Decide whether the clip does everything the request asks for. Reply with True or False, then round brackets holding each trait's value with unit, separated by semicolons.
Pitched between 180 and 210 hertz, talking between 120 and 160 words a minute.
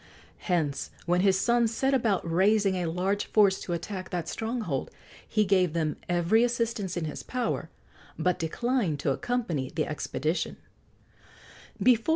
True (185 Hz; 140 wpm)